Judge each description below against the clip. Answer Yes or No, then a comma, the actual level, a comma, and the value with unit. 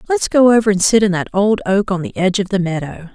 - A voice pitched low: No, high, 195 Hz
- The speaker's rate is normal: No, fast, 285 wpm